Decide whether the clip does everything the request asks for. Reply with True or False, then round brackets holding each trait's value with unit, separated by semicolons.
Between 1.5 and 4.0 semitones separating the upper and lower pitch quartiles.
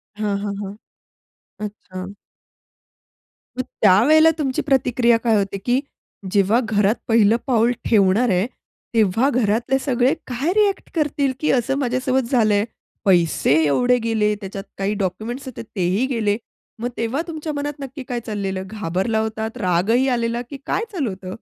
False (4.4 semitones)